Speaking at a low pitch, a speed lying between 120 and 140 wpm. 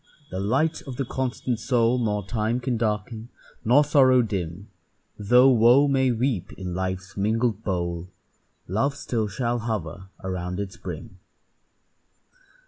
Yes: low, 110 Hz; slow, 135 wpm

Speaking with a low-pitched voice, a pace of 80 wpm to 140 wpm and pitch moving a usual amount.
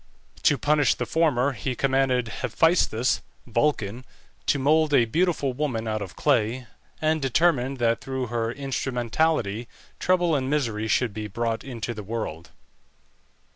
Yes: low, 125 Hz; slow, 135 wpm; average, 4.2 semitones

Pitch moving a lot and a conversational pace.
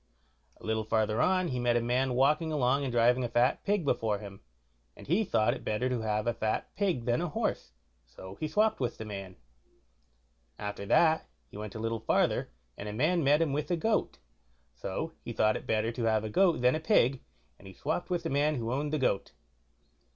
No: wide, 5.8 semitones; fast, 215 wpm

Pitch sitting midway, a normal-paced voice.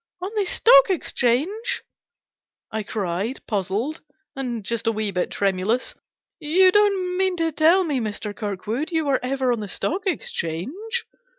No: very high, 270 Hz; average, 165 wpm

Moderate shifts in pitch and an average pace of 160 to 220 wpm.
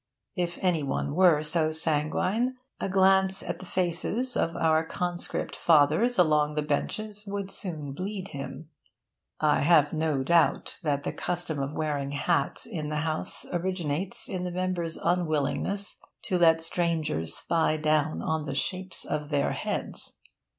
No: average, 3.3 semitones; average, 150 wpm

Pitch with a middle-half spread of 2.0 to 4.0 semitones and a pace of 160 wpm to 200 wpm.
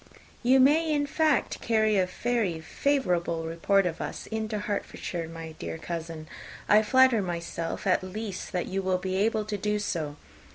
No: average, 4.6 semitones; average, 165 wpm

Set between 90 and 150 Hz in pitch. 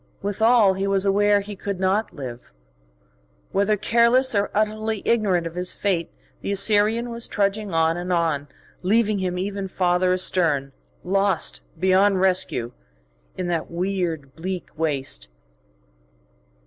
No: high, 190 Hz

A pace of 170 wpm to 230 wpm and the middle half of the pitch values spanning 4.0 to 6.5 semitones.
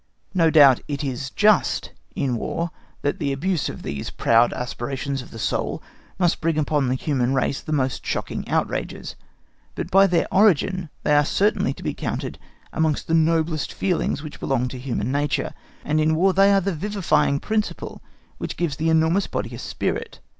Yes: average, 180 wpm; average, 4.4 semitones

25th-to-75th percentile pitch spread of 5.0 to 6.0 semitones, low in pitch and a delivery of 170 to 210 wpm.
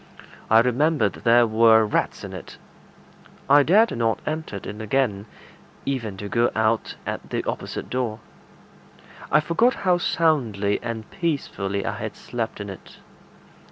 No: wide, 5.6 semitones; low, 115 Hz; average, 140 wpm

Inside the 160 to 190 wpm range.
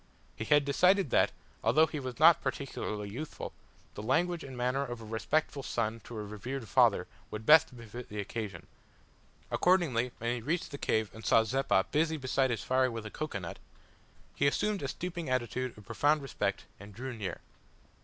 Yes: average, 185 wpm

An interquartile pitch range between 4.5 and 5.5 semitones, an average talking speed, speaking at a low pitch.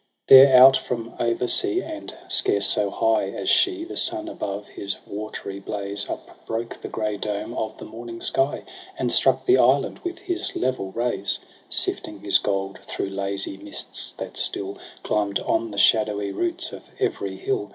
Yes: average, 5.1 semitones; average, 170 wpm; low, 110 Hz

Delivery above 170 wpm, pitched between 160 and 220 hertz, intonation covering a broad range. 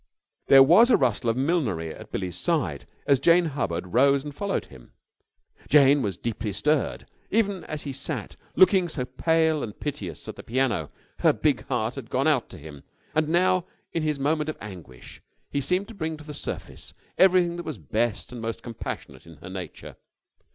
No: average, 185 wpm; medium, 140 Hz; wide, 7.4 semitones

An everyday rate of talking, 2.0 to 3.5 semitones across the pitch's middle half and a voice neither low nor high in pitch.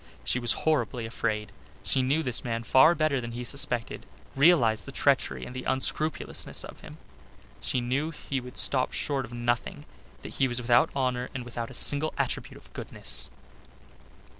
No: average, 170 wpm; average, 2.7 semitones; low, 125 Hz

